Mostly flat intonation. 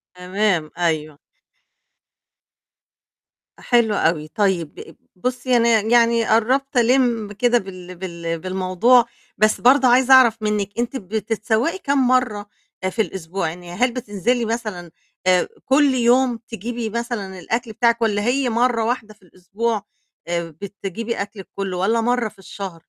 No: average, 4.3 semitones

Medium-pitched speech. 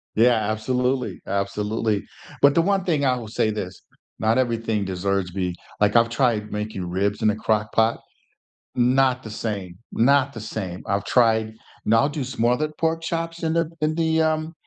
No: low, 115 Hz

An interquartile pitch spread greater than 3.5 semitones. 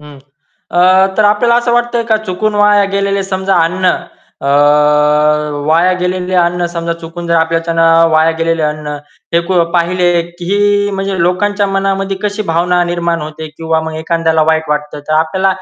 No: average, 3.2 semitones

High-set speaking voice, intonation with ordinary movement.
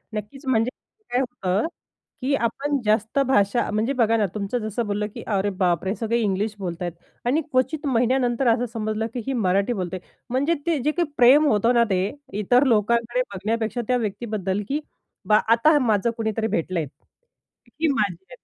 Yes: high, 225 Hz; average, 3.6 semitones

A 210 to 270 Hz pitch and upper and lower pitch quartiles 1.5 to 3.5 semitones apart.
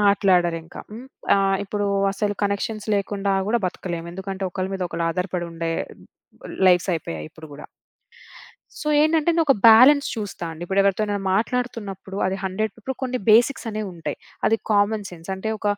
No: high, 200 Hz; average, 3.1 semitones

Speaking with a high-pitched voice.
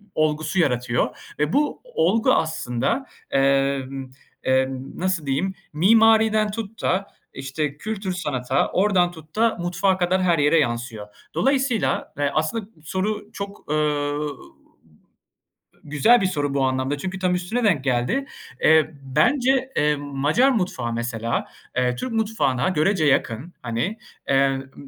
No: medium, 160 Hz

